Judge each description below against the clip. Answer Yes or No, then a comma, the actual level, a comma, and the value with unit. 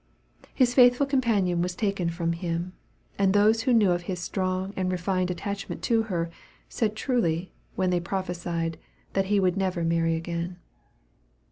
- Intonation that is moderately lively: Yes, average, 3.0 semitones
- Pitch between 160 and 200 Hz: Yes, medium, 185 Hz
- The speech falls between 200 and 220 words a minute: No, average, 155 wpm